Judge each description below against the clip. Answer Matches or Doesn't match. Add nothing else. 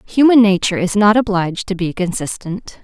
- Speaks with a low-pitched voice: Doesn't match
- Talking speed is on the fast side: Doesn't match